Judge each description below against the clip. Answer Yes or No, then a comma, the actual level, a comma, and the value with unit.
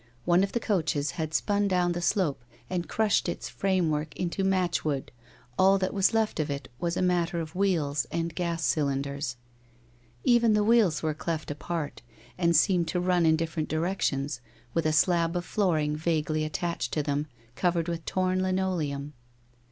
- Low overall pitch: No, medium, 170 Hz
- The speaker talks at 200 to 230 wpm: No, average, 175 wpm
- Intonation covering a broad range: No, average, 3.3 semitones